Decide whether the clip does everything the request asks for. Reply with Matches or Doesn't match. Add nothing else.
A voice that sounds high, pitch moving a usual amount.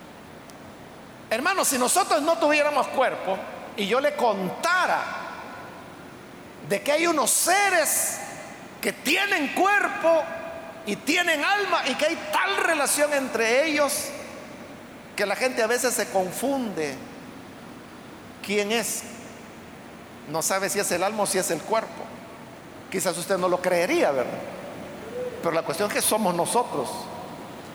Doesn't match